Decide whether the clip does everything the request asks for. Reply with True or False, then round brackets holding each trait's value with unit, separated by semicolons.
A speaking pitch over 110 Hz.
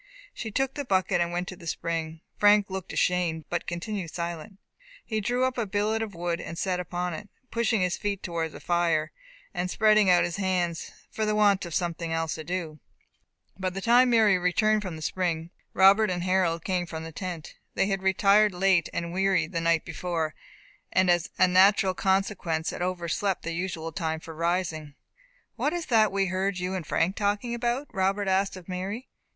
True (185 Hz)